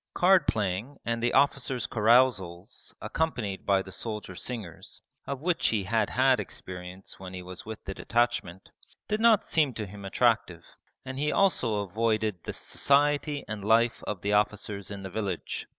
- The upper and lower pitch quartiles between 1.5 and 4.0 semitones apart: No, average, 5.0 semitones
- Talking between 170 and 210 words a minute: No, average, 160 wpm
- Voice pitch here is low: Yes, low, 110 Hz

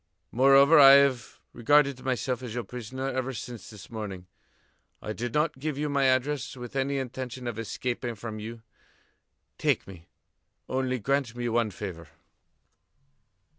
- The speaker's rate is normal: Yes, average, 145 wpm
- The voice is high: No, low, 125 Hz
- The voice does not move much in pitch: No, average, 3.1 semitones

